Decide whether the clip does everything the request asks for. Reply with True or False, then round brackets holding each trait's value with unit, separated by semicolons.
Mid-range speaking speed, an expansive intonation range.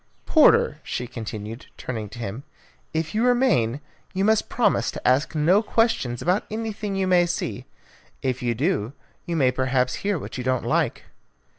True (165 wpm; 8.0 semitones)